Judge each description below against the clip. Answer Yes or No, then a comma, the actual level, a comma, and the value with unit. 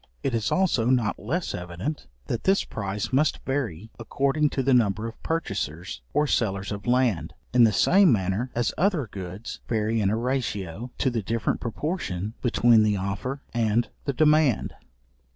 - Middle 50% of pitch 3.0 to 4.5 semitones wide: No, average, 5.0 semitones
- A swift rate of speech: No, average, 165 wpm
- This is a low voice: Yes, low, 115 Hz